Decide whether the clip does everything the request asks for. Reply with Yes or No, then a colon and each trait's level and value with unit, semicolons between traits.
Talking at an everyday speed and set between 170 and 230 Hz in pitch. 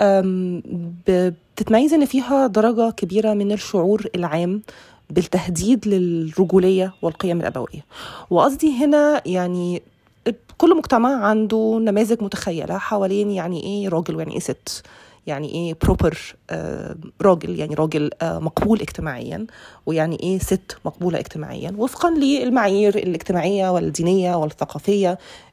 Yes: average, 110 wpm; high, 190 Hz